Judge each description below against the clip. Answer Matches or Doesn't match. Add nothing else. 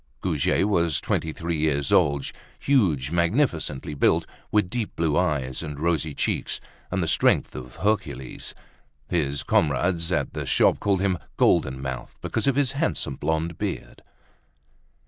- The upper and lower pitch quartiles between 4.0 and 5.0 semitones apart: Matches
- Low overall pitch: Matches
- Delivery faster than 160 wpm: Doesn't match